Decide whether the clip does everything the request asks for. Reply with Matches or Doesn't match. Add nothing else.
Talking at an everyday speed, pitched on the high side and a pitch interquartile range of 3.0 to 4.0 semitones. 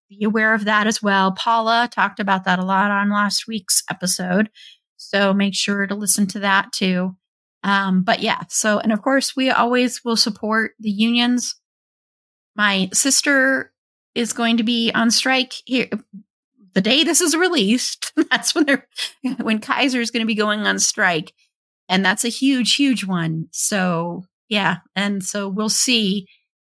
Matches